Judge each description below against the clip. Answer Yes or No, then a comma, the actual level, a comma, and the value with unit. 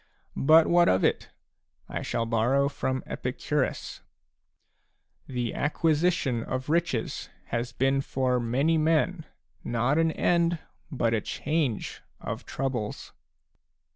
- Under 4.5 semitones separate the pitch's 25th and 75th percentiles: No, average, 5.1 semitones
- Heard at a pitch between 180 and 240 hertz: No, low, 135 Hz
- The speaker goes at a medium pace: No, slow, 120 wpm